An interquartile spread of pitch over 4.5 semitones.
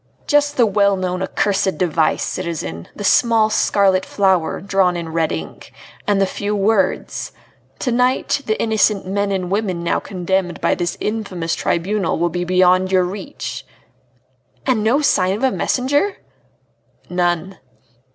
No: average, 3.2 semitones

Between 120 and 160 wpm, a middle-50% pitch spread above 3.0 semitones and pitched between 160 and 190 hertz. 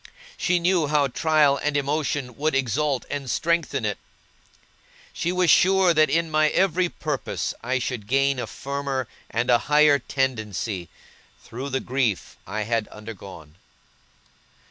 No: average, 140 wpm; average, 4.3 semitones; medium, 140 Hz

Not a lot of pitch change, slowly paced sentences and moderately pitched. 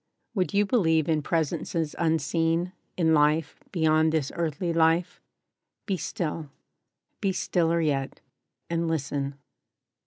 Yes: narrow, 1.6 semitones; slow, 115 wpm; medium, 160 Hz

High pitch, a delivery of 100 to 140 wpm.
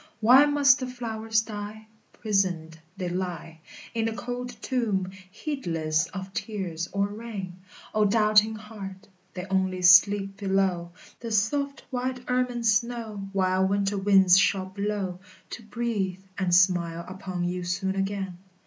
Yes: high, 200 Hz; slow, 135 wpm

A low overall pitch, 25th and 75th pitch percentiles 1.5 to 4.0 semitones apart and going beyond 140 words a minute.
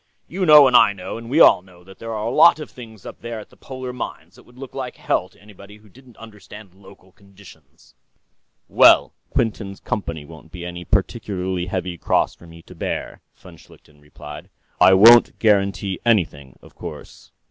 No: low, 100 Hz; average, 4.5 semitones; average, 195 wpm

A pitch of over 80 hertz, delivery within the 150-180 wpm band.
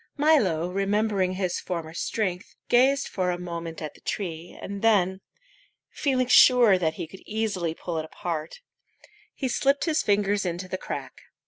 Yes: high, 190 Hz; average, 155 wpm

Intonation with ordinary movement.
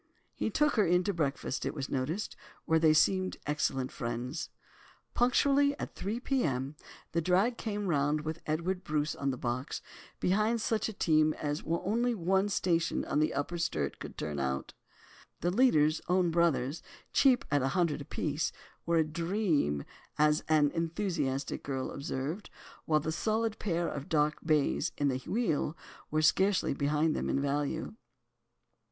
Yes: average, 4.8 semitones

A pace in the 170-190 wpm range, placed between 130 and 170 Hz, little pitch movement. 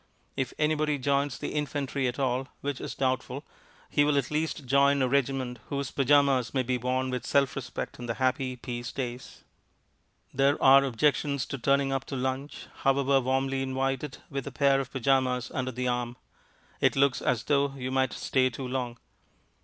Yes: average, 175 wpm; low, 135 Hz; narrow, 1.6 semitones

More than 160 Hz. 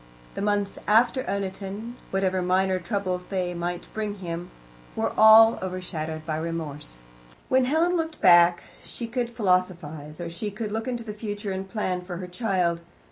Yes: high, 190 Hz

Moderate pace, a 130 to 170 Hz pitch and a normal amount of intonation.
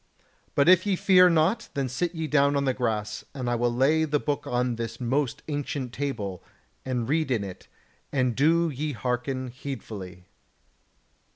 Yes: average, 170 wpm; low, 135 Hz; average, 4.0 semitones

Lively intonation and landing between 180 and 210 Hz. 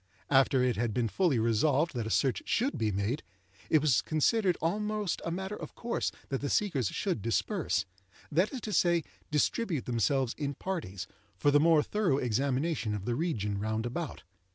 No: wide, 7.2 semitones; medium, 140 Hz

